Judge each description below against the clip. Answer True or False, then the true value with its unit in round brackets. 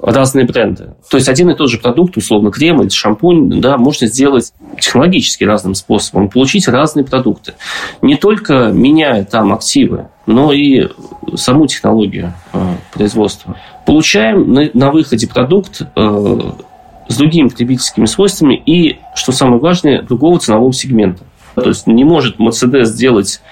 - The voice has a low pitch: True (130 Hz)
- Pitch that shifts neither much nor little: False (6.6 semitones)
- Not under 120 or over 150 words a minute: True (135 wpm)